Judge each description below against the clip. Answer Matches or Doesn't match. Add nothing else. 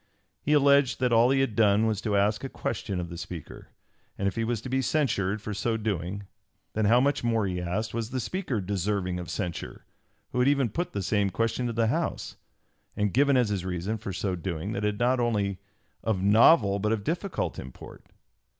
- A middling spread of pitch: Matches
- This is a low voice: Matches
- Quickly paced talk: Matches